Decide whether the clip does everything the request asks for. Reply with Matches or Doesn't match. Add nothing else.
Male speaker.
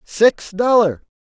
Matches